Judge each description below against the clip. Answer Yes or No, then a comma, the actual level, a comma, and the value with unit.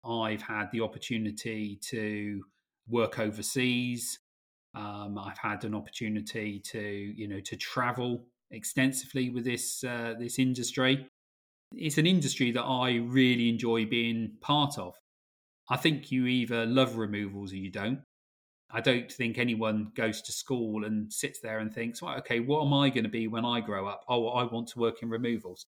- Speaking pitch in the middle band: No, low, 115 Hz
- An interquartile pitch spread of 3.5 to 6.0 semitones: No, average, 2.9 semitones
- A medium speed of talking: Yes, average, 170 wpm